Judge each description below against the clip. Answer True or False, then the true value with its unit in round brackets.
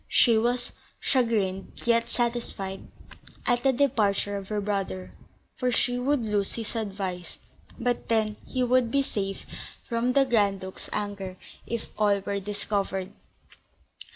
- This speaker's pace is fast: False (135 wpm)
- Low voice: False (215 Hz)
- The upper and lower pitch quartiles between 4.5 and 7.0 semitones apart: False (3.5 semitones)